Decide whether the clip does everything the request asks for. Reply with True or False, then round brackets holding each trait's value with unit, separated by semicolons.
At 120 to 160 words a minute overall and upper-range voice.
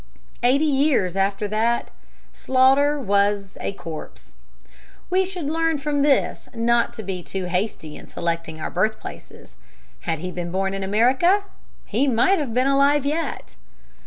True (145 wpm; 235 Hz)